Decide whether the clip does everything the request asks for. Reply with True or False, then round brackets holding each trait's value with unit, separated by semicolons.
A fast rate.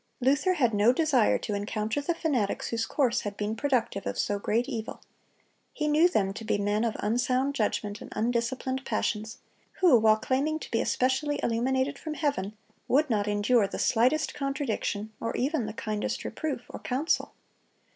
False (170 wpm)